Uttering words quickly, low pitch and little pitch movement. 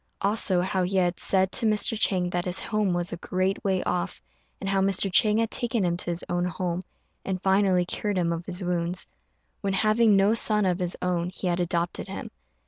No: fast, 215 wpm; medium, 185 Hz; narrow, 2.0 semitones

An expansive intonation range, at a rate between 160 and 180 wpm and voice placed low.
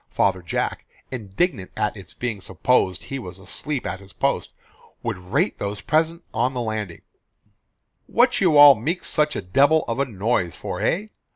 Yes: wide, 7.7 semitones; average, 170 wpm; low, 120 Hz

